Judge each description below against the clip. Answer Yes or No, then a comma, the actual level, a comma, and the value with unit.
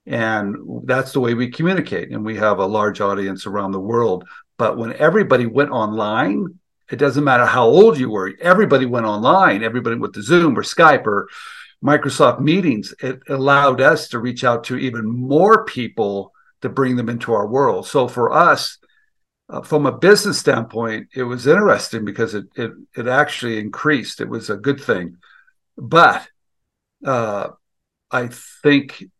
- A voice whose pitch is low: Yes, low, 125 Hz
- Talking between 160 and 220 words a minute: Yes, average, 165 wpm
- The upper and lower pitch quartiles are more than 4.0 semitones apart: Yes, average, 4.5 semitones